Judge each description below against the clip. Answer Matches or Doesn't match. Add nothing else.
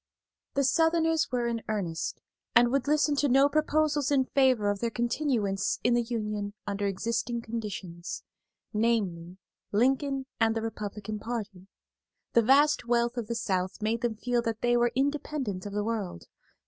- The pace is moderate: Matches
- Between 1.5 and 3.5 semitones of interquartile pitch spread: Doesn't match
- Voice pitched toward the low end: Doesn't match